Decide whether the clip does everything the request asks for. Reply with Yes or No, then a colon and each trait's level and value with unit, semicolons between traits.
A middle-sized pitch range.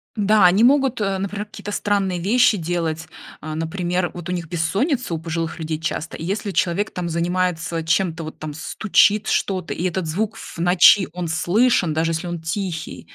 Yes: average, 3.5 semitones